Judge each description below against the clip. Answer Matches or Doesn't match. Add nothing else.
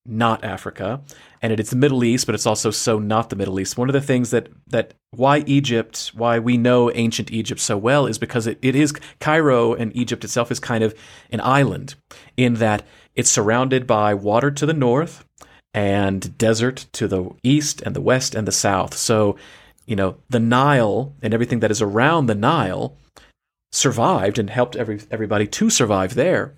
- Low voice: Matches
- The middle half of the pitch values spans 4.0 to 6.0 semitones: Doesn't match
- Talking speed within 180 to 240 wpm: Matches